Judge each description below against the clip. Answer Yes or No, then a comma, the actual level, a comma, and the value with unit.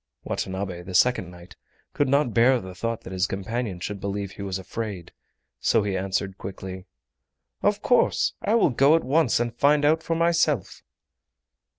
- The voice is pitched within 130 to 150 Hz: No, low, 105 Hz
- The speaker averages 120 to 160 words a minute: No, average, 170 wpm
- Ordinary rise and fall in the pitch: No, wide, 7.0 semitones